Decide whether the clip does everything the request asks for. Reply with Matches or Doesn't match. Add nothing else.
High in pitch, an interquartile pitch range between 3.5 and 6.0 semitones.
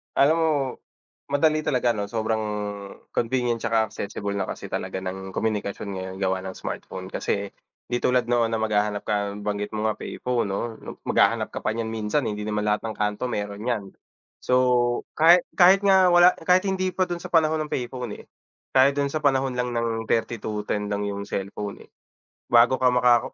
Doesn't match